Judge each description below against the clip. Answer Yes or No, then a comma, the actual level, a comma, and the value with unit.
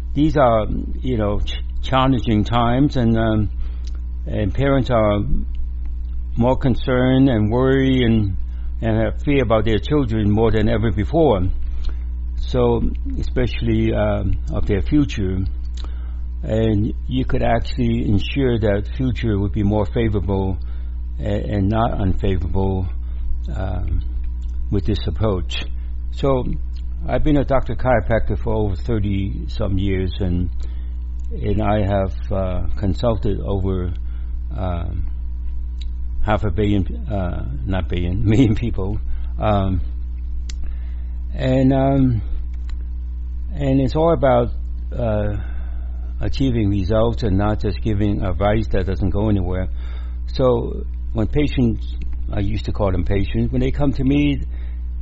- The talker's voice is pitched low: Yes, very low, 95 Hz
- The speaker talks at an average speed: No, slow, 120 wpm